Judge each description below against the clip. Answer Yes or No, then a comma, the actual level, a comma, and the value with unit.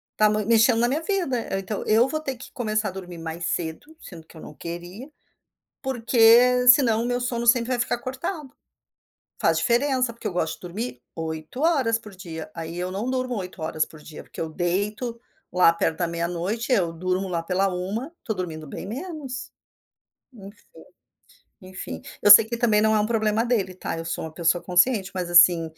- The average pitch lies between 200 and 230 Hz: Yes, high, 210 Hz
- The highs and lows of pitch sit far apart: Yes, wide, 5.8 semitones